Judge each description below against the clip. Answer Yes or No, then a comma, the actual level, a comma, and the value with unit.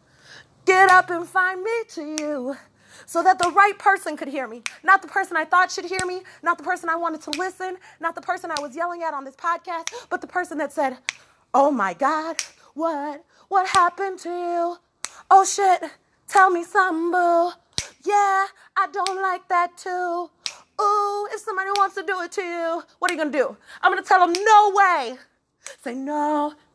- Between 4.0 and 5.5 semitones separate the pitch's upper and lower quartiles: No, average, 2.9 semitones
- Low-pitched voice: No, very high, 355 Hz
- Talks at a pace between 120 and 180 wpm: No, average, 190 wpm